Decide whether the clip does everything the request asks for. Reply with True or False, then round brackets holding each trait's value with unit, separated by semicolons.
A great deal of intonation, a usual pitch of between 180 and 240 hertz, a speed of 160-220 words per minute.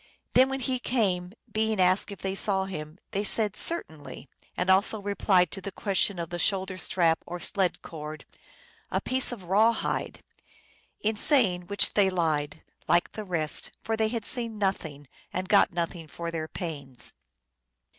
False (3.9 semitones; 190 Hz; 170 wpm)